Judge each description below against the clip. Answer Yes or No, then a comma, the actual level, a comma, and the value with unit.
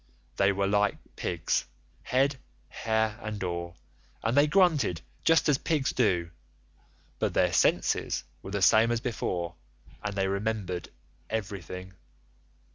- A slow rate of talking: Yes, slow, 120 wpm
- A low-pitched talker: Yes, low, 105 Hz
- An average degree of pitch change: Yes, average, 4.5 semitones